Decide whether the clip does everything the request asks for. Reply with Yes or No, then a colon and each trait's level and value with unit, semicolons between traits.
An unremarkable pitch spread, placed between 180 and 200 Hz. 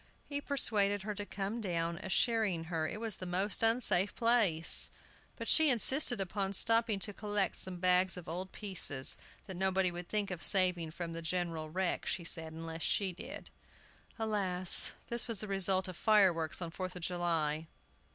Yes: average, 3.4 semitones; medium, 185 Hz